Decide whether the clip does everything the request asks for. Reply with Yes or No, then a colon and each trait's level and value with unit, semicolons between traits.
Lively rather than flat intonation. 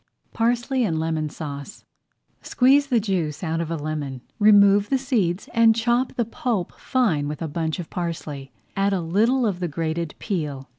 Yes: wide, 6.5 semitones